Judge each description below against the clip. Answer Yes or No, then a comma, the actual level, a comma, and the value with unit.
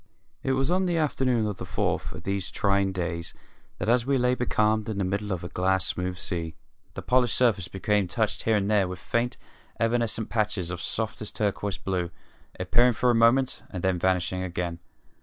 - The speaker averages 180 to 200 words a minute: Yes, average, 195 wpm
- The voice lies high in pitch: No, low, 105 Hz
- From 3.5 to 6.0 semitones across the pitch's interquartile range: Yes, average, 4.3 semitones